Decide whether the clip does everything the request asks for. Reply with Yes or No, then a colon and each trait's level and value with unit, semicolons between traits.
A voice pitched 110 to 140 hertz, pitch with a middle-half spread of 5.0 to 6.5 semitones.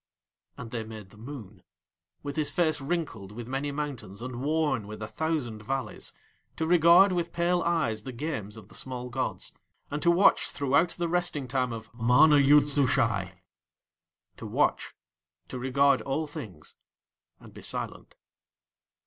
Yes: low, 135 Hz; wide, 5.6 semitones